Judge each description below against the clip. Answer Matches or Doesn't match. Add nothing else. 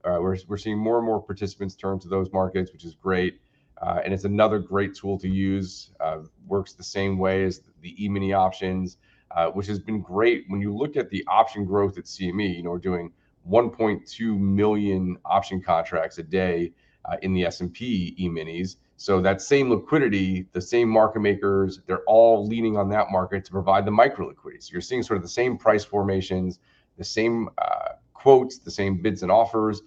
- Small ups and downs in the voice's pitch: Matches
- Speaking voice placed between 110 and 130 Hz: Doesn't match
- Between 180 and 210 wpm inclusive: Matches